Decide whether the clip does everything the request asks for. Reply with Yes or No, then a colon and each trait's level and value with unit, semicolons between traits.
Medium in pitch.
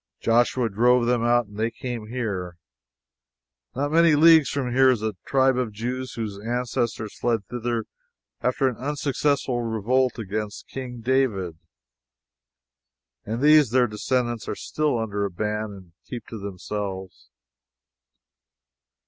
No: low, 120 Hz